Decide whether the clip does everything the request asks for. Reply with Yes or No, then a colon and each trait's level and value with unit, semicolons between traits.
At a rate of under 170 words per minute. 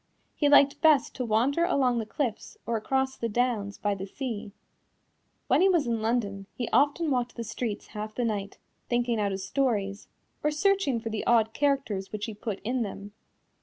No: average, 190 wpm